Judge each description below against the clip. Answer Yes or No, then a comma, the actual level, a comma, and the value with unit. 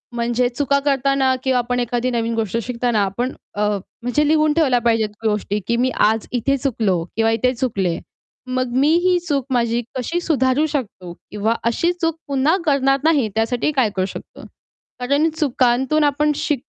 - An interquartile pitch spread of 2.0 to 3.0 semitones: No, average, 3.5 semitones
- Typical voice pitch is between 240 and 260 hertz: Yes, very high, 250 Hz